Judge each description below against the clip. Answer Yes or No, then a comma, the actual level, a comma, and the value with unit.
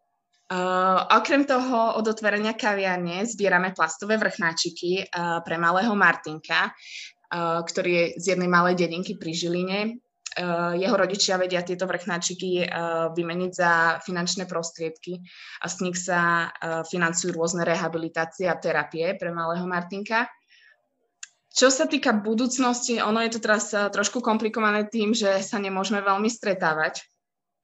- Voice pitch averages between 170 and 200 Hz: Yes, medium, 185 Hz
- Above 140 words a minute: No, average, 135 wpm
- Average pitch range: Yes, average, 3.8 semitones